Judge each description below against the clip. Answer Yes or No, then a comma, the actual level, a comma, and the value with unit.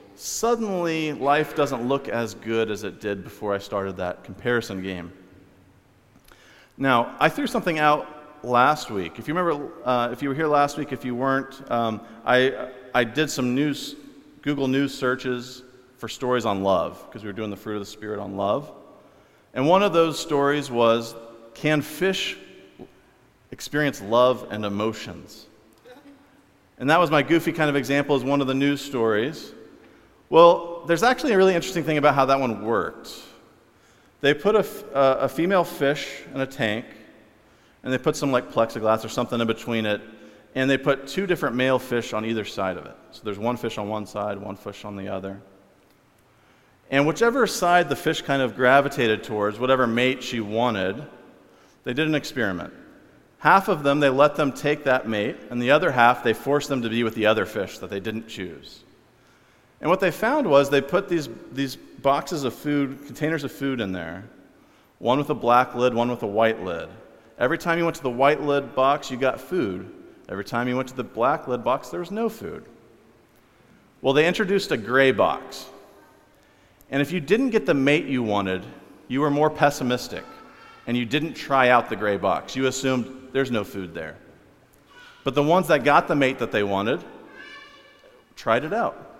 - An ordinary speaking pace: Yes, average, 190 wpm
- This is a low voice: Yes, low, 130 Hz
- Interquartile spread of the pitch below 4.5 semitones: No, average, 4.8 semitones